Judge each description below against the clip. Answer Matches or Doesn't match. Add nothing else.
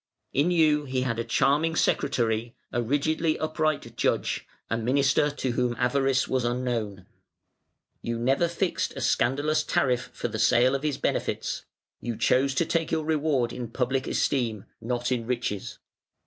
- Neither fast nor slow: Matches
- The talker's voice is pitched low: Matches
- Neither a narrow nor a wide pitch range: Matches